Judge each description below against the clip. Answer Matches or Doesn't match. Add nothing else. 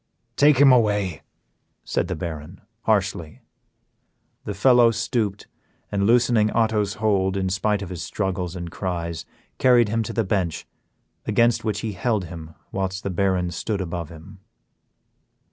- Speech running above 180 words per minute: Doesn't match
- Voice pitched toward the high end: Doesn't match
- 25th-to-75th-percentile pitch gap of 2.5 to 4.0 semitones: Matches